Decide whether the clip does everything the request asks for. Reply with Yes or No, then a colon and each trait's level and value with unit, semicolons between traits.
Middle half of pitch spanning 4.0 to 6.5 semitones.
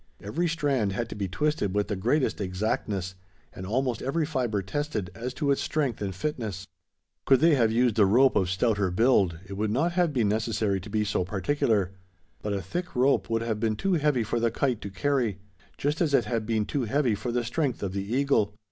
Yes: wide, 5.4 semitones